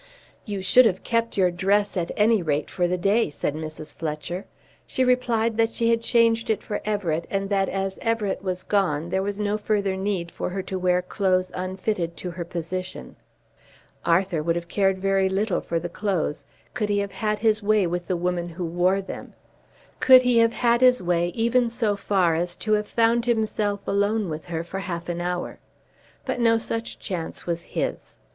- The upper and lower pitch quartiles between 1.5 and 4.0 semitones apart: Yes, average, 3.6 semitones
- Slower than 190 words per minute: No, average, 195 wpm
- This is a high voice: Yes, high, 195 Hz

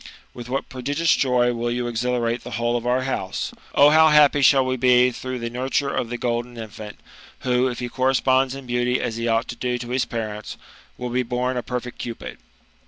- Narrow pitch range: Yes, narrow, 1.4 semitones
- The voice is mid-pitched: No, low, 125 Hz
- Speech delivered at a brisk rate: Yes, fast, 215 wpm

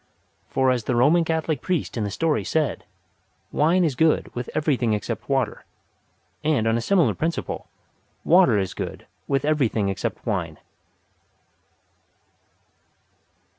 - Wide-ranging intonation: Yes, wide, 6.0 semitones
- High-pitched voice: No, low, 135 Hz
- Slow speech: Yes, slow, 130 wpm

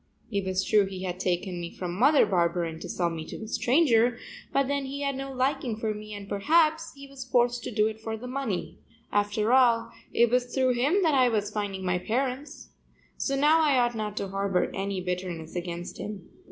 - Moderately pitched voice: No, high, 220 Hz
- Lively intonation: Yes, wide, 5.7 semitones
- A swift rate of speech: Yes, fast, 210 wpm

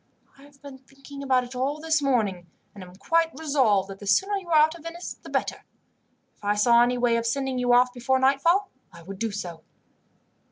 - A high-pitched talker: Yes, very high, 260 Hz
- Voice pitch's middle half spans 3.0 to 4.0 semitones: No, average, 4.8 semitones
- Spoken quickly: Yes, fast, 215 wpm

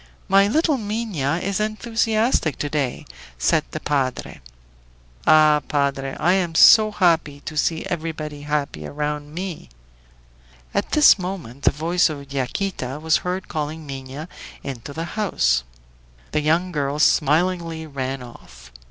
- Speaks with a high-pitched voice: No, medium, 155 Hz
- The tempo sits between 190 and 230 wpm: No, slow, 135 wpm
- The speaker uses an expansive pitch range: No, average, 4.6 semitones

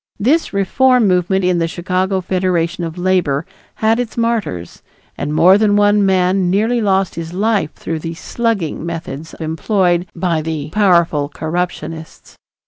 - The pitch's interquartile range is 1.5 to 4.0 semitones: Yes, average, 3.7 semitones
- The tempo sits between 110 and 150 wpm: Yes, average, 140 wpm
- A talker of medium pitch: Yes, medium, 180 Hz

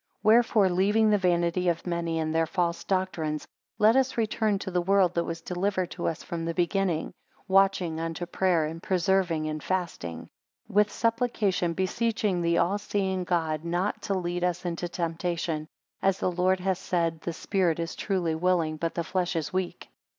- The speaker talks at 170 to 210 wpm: Yes, average, 180 wpm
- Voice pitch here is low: No, medium, 180 Hz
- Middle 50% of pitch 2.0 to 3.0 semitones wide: Yes, narrow, 2.5 semitones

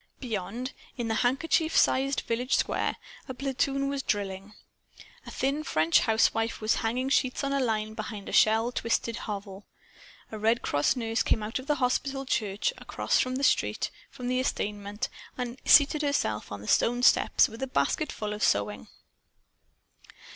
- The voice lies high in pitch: Yes, high, 230 Hz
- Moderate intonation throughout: Yes, average, 3.9 semitones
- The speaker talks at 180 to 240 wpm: No, average, 160 wpm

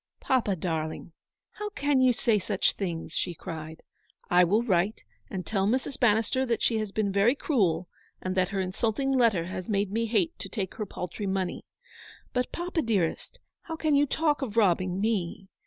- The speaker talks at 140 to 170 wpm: No, average, 190 wpm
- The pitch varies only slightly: No, average, 4.9 semitones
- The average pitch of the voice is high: Yes, high, 205 Hz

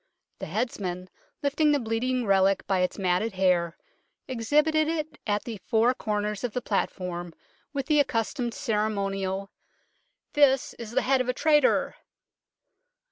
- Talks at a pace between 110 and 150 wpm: Yes, average, 145 wpm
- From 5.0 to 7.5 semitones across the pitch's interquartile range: Yes, wide, 5.6 semitones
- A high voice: Yes, high, 225 Hz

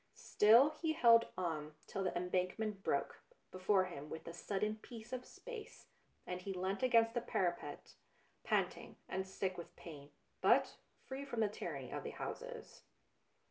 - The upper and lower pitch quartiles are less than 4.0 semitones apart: No, average, 4.6 semitones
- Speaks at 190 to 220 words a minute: No, average, 155 wpm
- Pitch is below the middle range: No, high, 195 Hz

